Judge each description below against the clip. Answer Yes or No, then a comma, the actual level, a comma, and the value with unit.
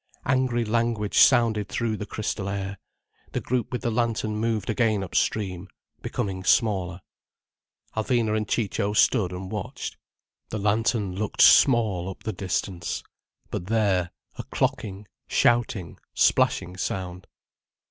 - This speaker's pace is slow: Yes, slow, 120 wpm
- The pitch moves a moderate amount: Yes, average, 3.2 semitones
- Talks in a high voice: No, low, 105 Hz